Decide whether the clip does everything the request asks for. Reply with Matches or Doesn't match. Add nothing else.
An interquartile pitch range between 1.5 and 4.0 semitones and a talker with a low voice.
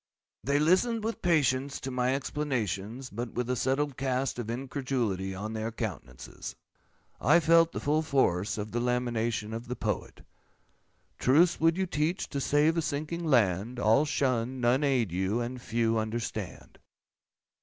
Doesn't match